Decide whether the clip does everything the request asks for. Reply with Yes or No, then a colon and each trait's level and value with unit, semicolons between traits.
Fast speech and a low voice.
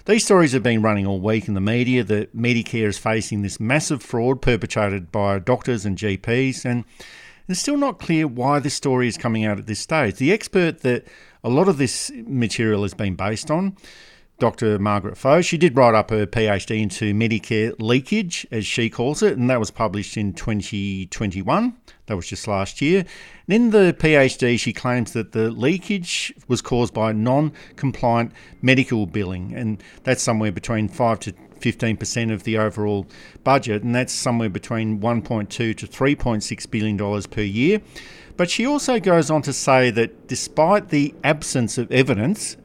No: average, 180 wpm; low, 120 Hz